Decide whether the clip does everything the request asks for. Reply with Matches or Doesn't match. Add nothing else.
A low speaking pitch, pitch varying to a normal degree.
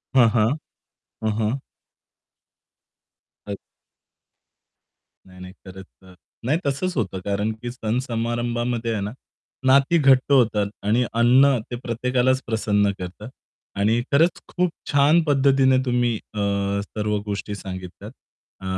Matches